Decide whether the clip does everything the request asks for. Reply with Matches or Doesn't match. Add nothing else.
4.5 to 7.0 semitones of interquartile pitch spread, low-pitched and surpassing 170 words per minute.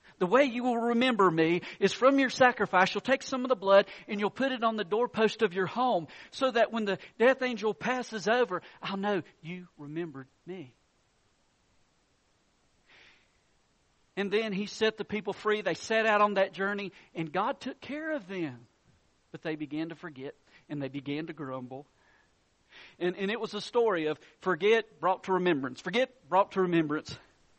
Doesn't match